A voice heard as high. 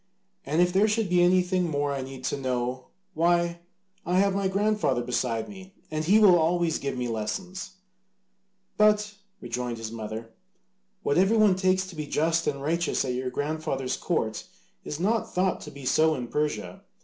No: medium, 160 Hz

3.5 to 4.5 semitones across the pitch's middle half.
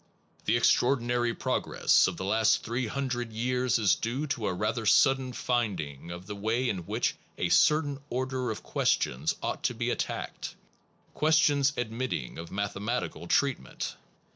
Yes: average, 4.2 semitones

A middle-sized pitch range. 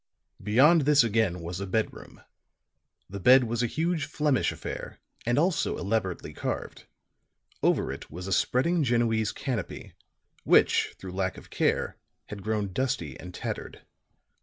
No: wide, 5.8 semitones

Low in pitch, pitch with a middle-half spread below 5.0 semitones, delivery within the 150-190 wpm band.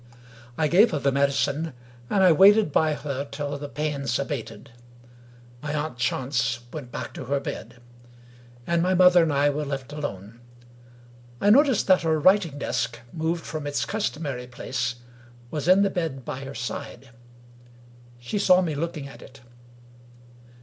No: medium, 145 Hz; average, 3.8 semitones; average, 155 wpm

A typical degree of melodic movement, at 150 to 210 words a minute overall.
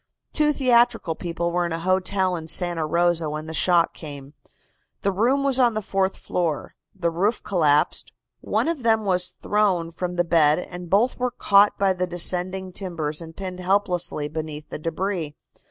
Yes: average, 3.3 semitones; average, 175 wpm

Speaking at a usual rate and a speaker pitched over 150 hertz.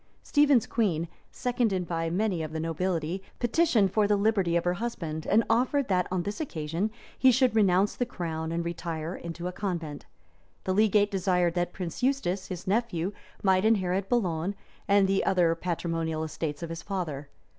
Yes: average, 170 wpm; medium, 185 Hz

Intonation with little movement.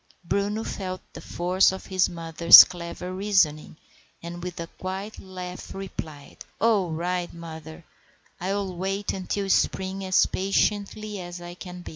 Yes: narrow, 2.0 semitones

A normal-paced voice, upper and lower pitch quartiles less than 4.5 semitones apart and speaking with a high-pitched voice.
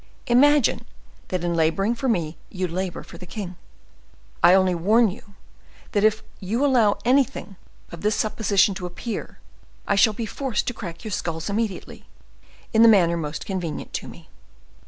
Yes: average, 165 wpm; average, 4.1 semitones; high, 200 Hz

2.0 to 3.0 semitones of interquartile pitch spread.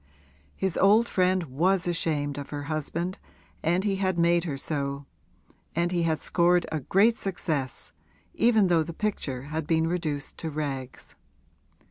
No: average, 3.9 semitones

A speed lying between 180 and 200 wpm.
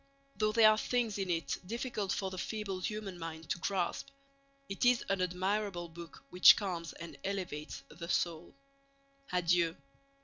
No: average, 150 wpm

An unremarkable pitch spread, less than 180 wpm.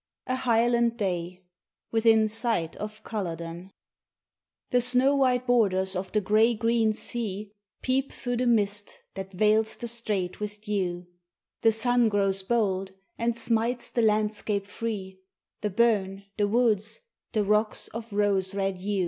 Yes: average, 3.1 semitones; average, 145 wpm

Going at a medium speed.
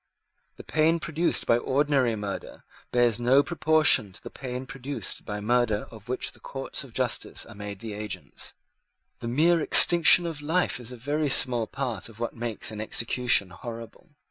Yes: average, 170 wpm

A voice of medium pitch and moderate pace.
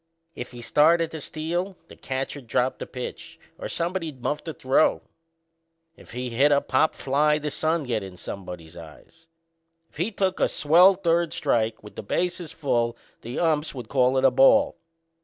Yes: medium, 145 Hz; average, 175 wpm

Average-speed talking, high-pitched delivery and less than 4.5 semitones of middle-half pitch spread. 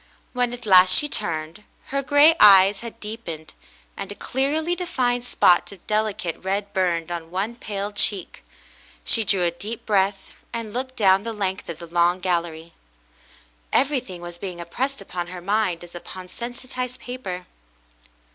No: average, 155 wpm; high, 200 Hz; wide, 5.5 semitones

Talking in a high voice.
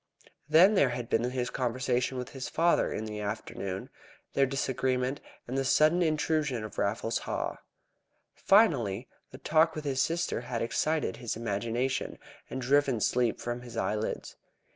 No: low, 125 Hz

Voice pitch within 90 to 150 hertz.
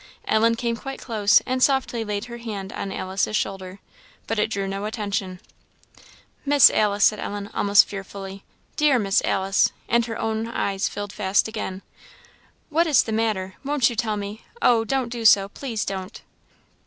No: high, 215 Hz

